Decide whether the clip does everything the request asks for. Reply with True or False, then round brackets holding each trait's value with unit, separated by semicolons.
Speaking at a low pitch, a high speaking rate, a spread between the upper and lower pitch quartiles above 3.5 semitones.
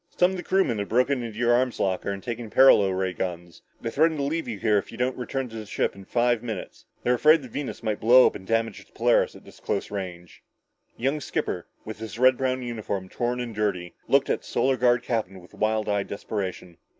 True (115 Hz; 235 wpm; 4.1 semitones)